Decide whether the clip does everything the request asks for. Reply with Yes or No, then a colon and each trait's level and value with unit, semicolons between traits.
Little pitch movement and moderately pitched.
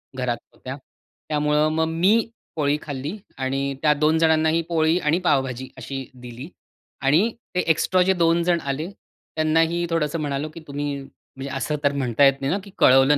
No: average, 3.2 semitones; medium, 150 Hz